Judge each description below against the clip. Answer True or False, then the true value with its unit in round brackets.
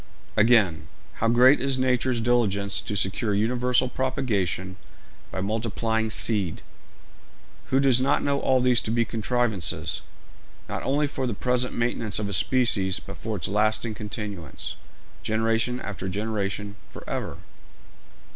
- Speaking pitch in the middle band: False (110 Hz)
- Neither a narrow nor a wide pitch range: True (3.6 semitones)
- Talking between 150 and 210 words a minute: False (135 wpm)